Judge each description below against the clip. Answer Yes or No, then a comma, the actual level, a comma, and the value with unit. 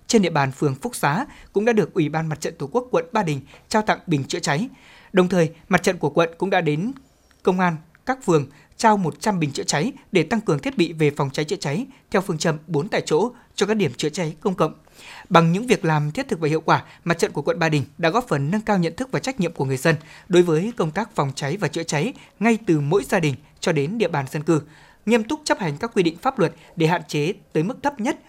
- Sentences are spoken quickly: Yes, fast, 270 wpm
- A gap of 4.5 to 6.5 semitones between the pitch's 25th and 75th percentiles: Yes, wide, 5.6 semitones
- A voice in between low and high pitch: Yes, medium, 170 Hz